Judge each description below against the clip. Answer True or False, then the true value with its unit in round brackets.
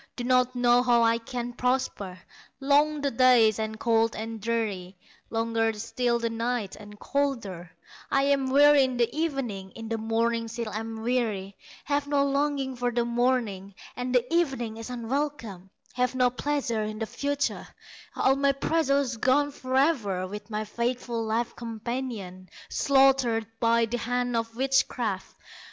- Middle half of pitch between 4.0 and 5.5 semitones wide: False (3.0 semitones)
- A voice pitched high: True (240 Hz)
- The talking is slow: False (150 wpm)